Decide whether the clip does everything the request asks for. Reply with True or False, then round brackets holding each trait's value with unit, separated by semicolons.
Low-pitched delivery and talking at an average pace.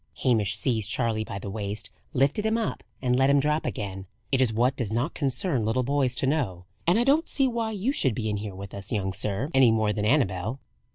False (125 Hz; 230 wpm)